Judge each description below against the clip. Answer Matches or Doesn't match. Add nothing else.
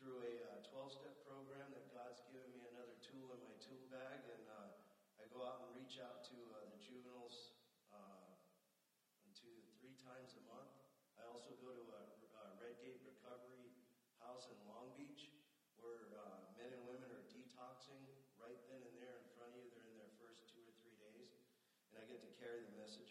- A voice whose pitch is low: Matches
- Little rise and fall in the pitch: Matches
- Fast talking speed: Doesn't match